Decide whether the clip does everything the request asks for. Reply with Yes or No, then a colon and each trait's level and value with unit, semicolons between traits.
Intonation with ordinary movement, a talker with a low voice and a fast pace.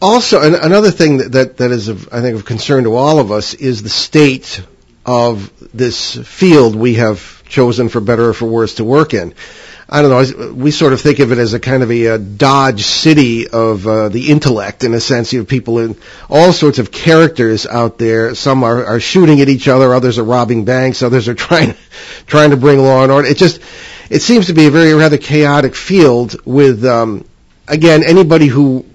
Yes: average, 4.2 semitones; low, 130 Hz; fast, 210 wpm